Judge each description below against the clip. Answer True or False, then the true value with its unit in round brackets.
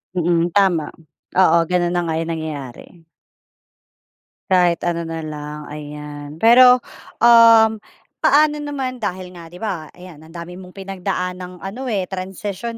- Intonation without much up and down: False (3.6 semitones)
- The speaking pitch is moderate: True (180 Hz)